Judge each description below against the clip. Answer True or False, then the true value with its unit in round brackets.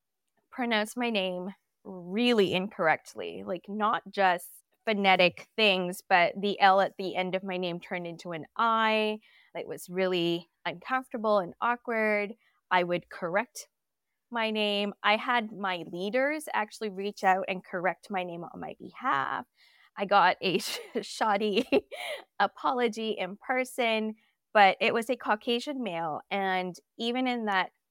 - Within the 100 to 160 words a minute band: True (140 wpm)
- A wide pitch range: False (3.4 semitones)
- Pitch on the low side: False (205 Hz)